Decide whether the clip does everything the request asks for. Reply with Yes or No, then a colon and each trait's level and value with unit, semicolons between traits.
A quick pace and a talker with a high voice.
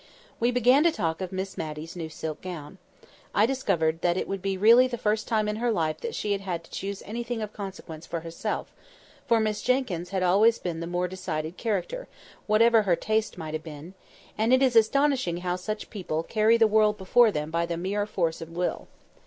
Yes: fast, 210 wpm; high, 195 Hz